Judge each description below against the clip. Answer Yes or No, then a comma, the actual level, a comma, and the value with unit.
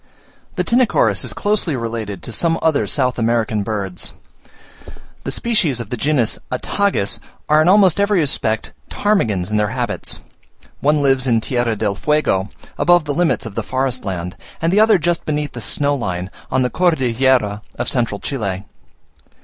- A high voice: No, low, 130 Hz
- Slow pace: No, average, 165 wpm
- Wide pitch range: Yes, wide, 6.8 semitones